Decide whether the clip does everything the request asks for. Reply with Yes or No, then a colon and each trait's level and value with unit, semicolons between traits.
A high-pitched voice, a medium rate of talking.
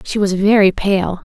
Yes: high, 195 Hz; average, 185 wpm